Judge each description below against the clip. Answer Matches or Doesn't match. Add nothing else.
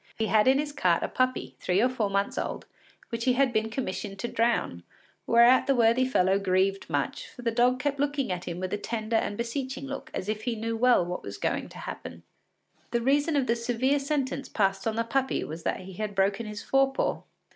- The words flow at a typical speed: Doesn't match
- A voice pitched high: Matches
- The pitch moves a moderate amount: Matches